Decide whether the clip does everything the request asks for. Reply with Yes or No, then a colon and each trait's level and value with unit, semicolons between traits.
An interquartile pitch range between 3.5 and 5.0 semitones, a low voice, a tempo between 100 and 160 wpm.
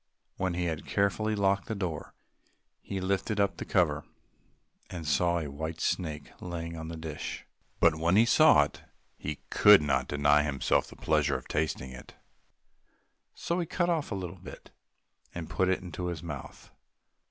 No: average, 4.1 semitones; very low, 85 Hz; average, 170 wpm